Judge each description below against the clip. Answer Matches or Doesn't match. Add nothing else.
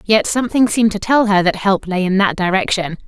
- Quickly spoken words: Matches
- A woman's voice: Matches